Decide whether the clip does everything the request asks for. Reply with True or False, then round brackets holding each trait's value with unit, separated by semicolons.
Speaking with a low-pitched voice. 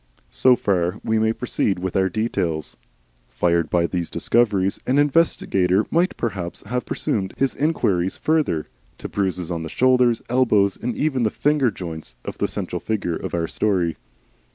True (100 Hz)